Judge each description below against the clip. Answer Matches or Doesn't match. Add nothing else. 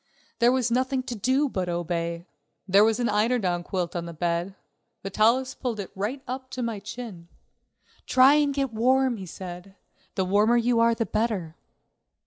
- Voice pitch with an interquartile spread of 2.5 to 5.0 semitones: Doesn't match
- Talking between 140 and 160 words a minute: Doesn't match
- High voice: Matches